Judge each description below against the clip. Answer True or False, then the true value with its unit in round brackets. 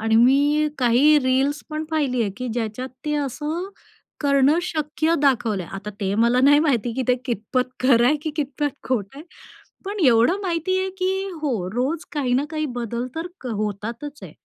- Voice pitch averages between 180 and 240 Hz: False (265 Hz)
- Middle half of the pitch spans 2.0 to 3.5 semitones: False (4.3 semitones)